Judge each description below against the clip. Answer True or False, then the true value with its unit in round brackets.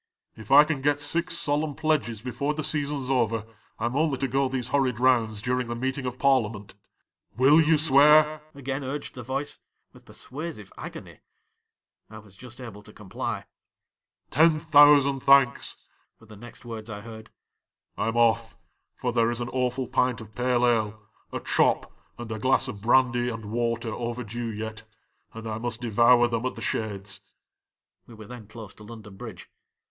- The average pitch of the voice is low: True (120 Hz)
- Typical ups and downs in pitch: True (3.7 semitones)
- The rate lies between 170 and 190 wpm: True (185 wpm)